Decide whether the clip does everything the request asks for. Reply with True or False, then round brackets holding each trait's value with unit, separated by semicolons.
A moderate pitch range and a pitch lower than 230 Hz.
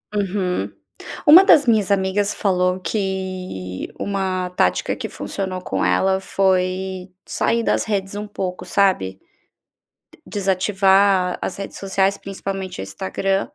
False (1.3 semitones; 190 Hz)